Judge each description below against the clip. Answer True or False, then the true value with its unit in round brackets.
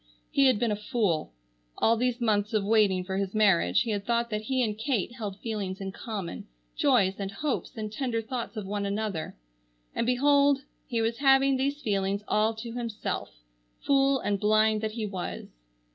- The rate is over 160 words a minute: True (185 wpm)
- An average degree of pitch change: True (3.3 semitones)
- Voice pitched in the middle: False (220 Hz)